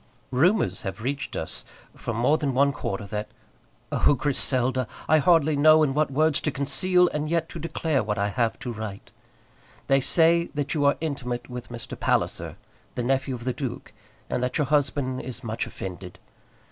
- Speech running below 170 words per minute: No, average, 185 wpm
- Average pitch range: Yes, average, 3.9 semitones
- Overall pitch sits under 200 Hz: Yes, low, 135 Hz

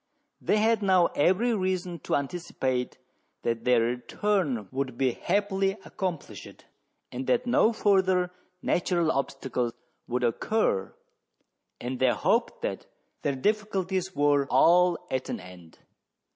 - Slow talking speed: Yes, slow, 120 wpm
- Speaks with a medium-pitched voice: Yes, medium, 170 Hz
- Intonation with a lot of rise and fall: Yes, wide, 7.1 semitones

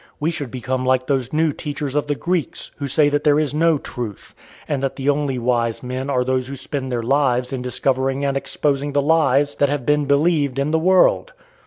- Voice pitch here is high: No, medium, 140 Hz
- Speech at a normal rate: No, fast, 215 wpm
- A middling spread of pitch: No, narrow, 2.3 semitones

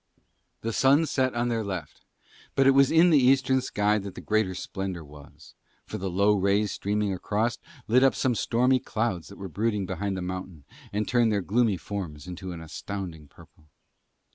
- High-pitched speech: No, low, 105 Hz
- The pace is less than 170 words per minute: No, average, 185 wpm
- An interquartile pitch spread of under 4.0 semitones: No, average, 4.4 semitones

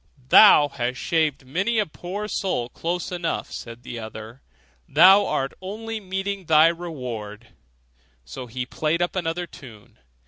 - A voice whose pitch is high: No, medium, 160 Hz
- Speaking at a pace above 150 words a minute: No, average, 140 wpm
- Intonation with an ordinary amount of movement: No, wide, 7.0 semitones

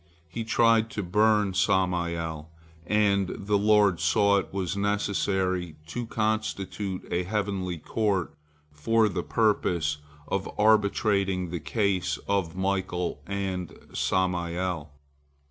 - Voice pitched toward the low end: Yes, very low, 95 Hz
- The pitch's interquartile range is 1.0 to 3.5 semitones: Yes, average, 2.7 semitones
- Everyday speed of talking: No, slow, 110 wpm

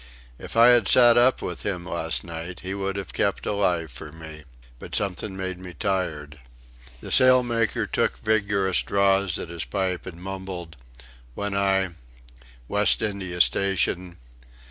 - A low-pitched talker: Yes, very low, 95 Hz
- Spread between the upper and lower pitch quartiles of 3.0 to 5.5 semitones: No, narrow, 2.6 semitones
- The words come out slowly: No, average, 145 wpm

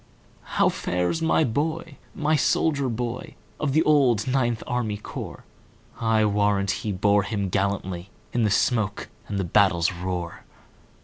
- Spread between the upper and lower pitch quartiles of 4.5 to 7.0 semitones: Yes, average, 4.9 semitones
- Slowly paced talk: Yes, slow, 120 wpm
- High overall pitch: No, low, 105 Hz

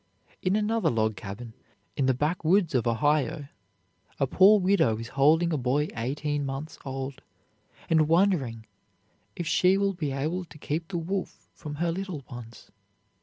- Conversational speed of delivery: Yes, average, 155 wpm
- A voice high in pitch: No, medium, 150 Hz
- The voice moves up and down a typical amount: Yes, average, 4.9 semitones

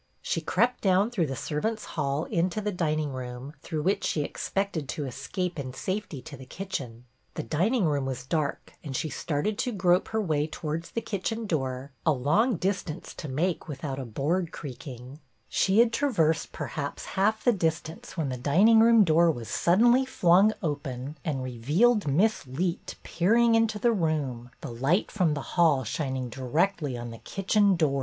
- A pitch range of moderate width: No, wide, 6.3 semitones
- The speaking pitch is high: No, medium, 160 Hz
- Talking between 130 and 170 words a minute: No, average, 180 wpm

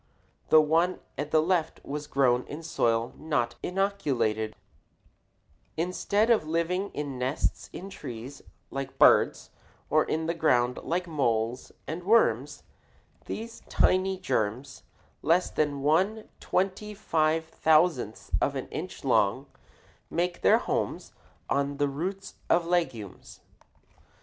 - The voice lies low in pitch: No, medium, 155 Hz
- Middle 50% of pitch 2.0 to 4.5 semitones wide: No, average, 4.9 semitones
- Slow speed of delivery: Yes, slow, 120 wpm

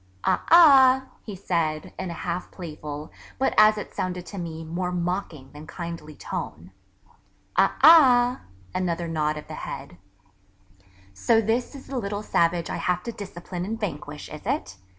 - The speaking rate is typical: Yes, average, 160 wpm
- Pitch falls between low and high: Yes, medium, 180 Hz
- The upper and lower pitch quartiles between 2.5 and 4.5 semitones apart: No, average, 5.2 semitones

